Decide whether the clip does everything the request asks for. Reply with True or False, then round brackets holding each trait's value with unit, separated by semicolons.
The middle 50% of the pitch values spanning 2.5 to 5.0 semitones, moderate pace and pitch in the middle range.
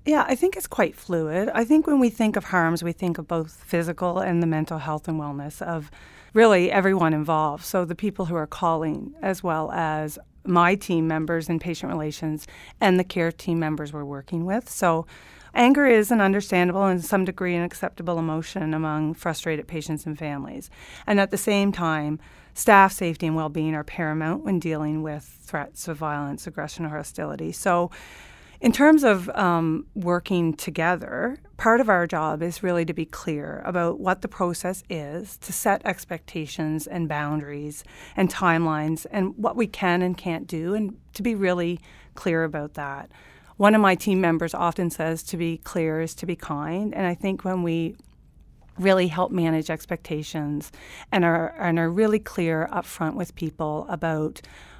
True (3.3 semitones; 180 wpm; 170 Hz)